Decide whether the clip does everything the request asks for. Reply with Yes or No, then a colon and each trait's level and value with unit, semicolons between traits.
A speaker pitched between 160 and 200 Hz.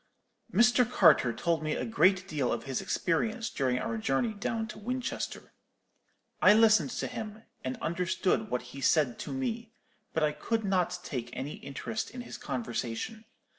Yes: medium, 185 Hz